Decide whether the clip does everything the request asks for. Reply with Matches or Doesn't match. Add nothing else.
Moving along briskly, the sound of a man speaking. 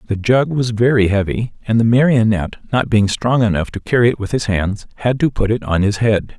Matches